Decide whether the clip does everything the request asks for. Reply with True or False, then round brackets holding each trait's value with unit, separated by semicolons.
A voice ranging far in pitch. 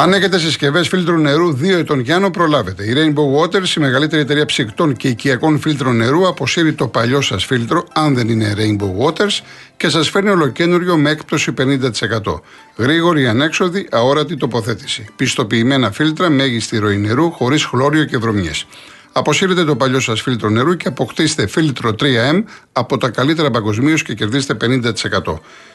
False (5.0 semitones)